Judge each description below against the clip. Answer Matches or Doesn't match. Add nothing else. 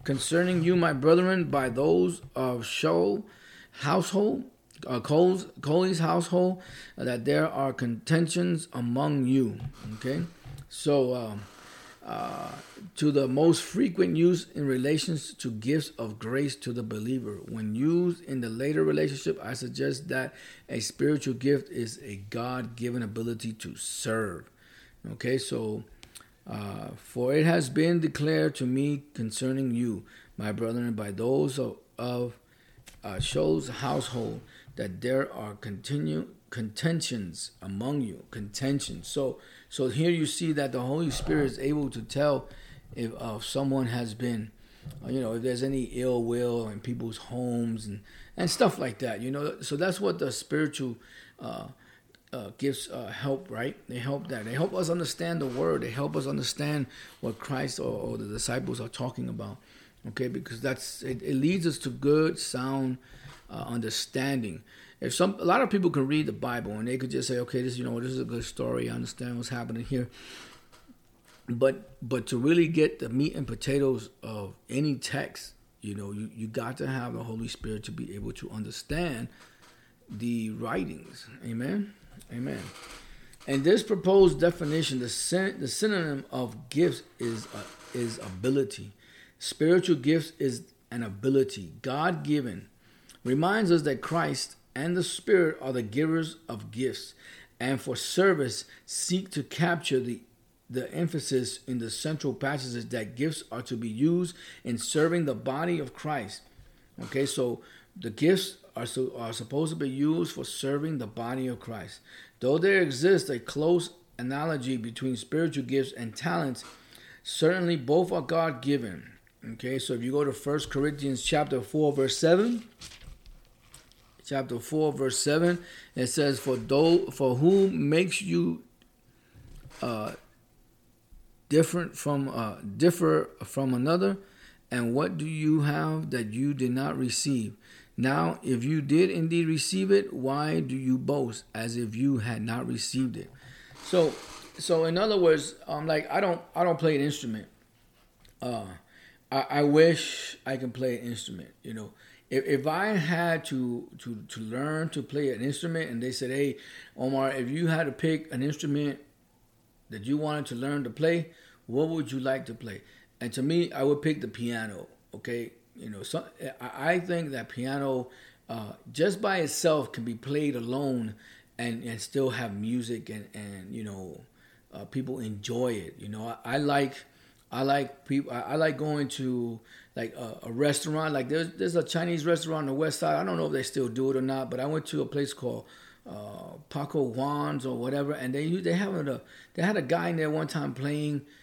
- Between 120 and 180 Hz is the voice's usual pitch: Matches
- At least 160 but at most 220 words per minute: Matches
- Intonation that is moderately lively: Matches